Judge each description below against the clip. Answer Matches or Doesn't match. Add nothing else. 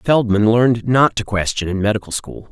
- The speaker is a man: Matches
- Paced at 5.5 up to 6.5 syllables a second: Doesn't match